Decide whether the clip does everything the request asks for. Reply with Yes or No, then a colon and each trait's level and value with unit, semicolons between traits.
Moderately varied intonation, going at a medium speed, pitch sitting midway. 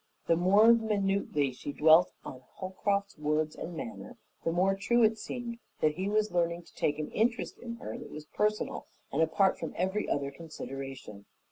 No: wide, 5.7 semitones; average, 175 wpm; medium, 180 Hz